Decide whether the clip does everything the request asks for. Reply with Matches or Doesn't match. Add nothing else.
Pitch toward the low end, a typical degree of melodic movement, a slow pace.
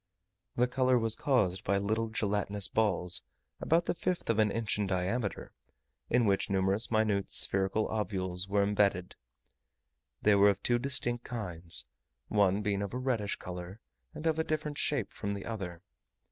Doesn't match